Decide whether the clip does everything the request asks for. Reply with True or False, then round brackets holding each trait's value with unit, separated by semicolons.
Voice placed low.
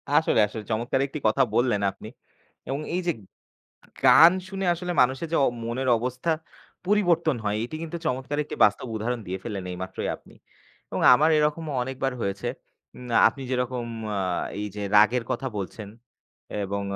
True (125 Hz)